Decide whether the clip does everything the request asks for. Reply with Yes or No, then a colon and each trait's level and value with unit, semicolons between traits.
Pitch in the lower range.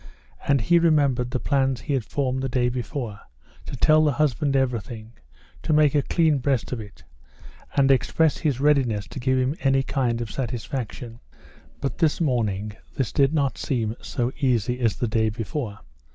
Yes: low, 130 Hz